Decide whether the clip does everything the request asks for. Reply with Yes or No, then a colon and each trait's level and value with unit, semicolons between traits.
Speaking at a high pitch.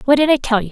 Yes: very high, 265 Hz